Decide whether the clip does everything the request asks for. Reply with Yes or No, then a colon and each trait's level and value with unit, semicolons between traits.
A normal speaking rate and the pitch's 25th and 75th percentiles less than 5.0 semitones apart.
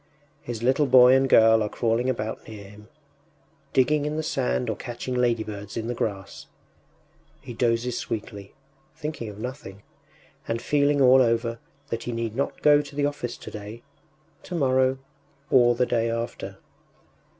Yes: average, 150 wpm; average, 2.8 semitones